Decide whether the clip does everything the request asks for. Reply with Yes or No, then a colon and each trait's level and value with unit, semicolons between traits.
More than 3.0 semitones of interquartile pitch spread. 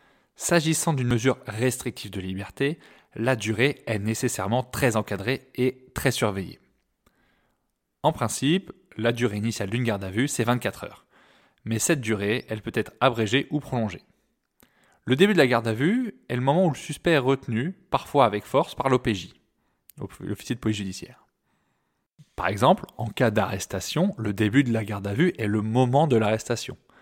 Yes: average, 4.1 semitones